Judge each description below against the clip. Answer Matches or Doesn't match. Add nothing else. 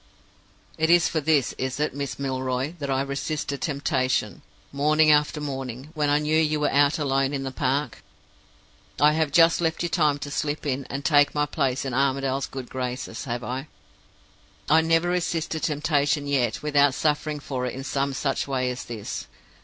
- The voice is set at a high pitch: Doesn't match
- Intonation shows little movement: Matches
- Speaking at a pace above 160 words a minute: Matches